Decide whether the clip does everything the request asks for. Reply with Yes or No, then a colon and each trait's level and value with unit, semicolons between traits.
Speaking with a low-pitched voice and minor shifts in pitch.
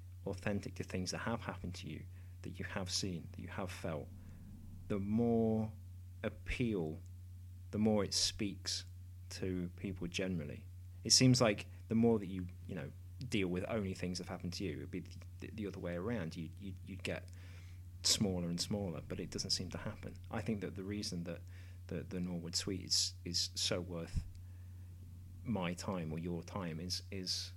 Yes: very low, 90 Hz; narrow, 1.6 semitones